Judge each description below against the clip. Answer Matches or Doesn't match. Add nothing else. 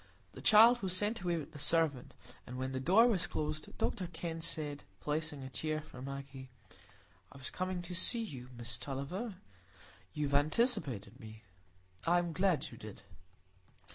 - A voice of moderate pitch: Matches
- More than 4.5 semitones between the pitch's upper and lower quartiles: Matches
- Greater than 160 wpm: Matches